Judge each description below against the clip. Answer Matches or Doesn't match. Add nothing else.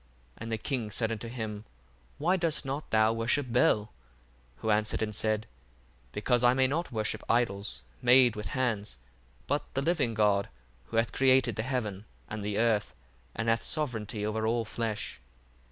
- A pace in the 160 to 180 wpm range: Matches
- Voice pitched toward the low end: Matches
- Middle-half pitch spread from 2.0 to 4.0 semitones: Matches